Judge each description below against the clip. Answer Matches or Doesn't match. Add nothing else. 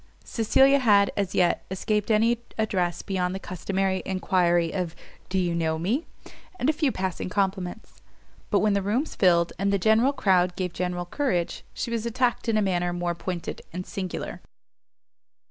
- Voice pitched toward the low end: Doesn't match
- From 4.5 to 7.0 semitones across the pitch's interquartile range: Doesn't match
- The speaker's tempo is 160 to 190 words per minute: Matches